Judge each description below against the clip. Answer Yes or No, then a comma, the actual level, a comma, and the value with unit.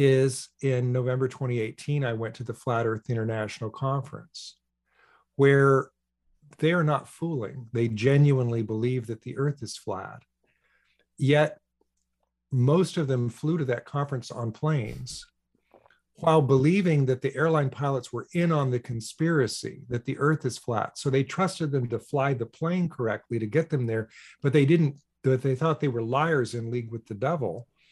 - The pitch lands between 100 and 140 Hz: Yes, low, 135 Hz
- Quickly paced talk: No, average, 165 wpm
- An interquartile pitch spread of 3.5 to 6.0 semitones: Yes, average, 4.1 semitones